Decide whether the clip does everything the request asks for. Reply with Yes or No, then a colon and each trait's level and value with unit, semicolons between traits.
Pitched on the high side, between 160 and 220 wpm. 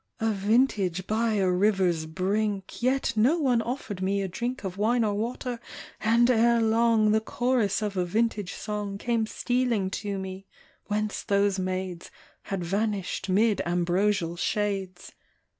No: high, 210 Hz; average, 145 wpm